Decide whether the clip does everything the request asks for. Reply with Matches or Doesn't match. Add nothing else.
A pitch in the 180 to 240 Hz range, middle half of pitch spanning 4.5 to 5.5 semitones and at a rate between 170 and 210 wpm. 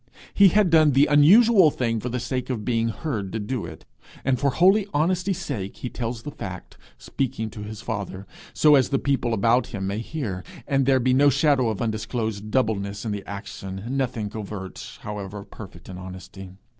Doesn't match